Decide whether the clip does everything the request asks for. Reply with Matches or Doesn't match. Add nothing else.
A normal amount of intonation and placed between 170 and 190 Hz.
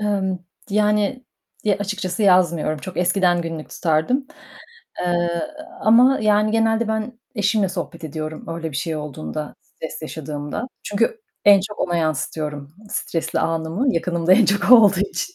Matches